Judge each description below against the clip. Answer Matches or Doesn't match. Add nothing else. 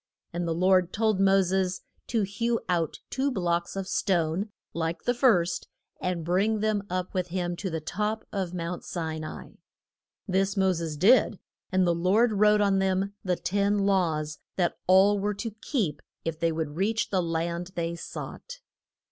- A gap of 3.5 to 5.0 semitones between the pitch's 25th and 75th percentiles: Doesn't match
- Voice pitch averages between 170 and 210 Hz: Matches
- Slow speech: Doesn't match